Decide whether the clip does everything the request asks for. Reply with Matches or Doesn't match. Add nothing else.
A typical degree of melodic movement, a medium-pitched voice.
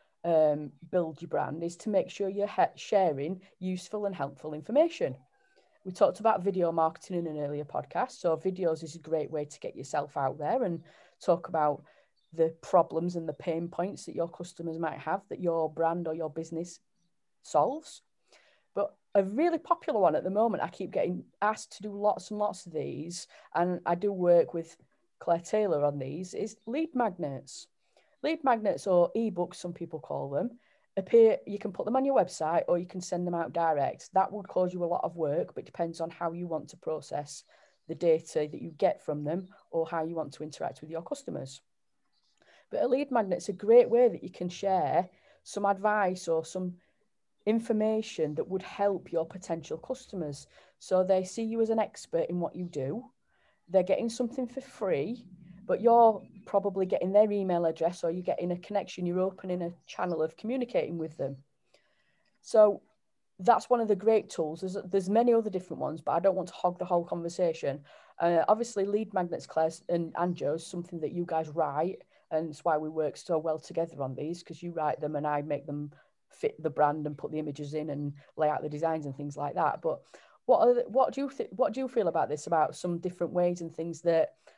Matches